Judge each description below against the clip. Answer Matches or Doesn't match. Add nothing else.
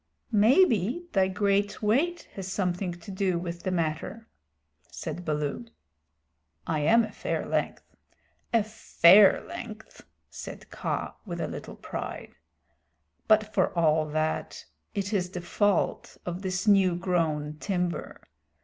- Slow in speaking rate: Matches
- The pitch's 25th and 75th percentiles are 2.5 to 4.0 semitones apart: Matches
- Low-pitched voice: Doesn't match